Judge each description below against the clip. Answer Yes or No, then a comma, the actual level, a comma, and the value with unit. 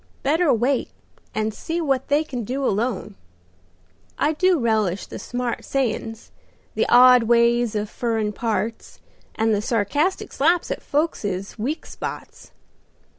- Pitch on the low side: No, high, 240 Hz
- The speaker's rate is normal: No, slow, 130 wpm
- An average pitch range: Yes, average, 4.4 semitones